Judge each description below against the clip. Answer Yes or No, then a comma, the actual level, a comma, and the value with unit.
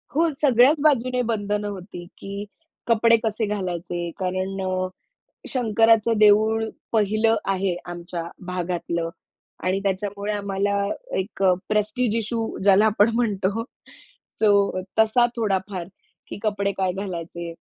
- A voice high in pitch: Yes, high, 205 Hz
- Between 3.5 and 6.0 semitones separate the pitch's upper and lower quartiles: No, average, 3.0 semitones